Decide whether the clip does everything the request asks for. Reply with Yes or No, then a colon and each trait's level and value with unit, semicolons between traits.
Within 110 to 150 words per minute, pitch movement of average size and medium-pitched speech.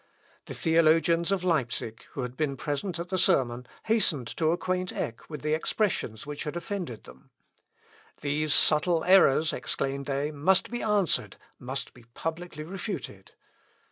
Yes: average, 145 wpm; average, 4.7 semitones; medium, 155 Hz